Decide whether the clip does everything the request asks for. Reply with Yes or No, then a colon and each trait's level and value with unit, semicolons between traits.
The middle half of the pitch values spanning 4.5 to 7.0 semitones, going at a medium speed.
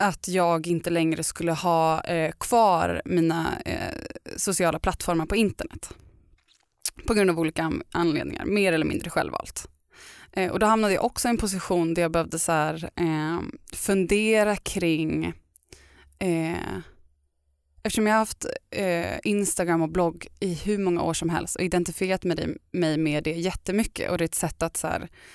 No: average, 3.4 semitones; average, 165 wpm